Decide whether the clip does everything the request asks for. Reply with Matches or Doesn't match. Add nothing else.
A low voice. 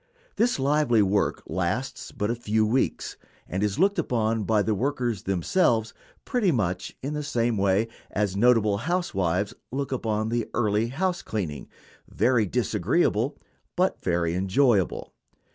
Matches